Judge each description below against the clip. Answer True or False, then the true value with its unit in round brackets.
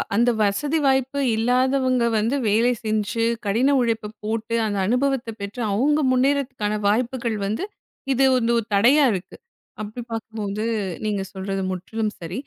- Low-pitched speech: False (225 Hz)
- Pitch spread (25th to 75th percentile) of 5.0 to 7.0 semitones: False (3.6 semitones)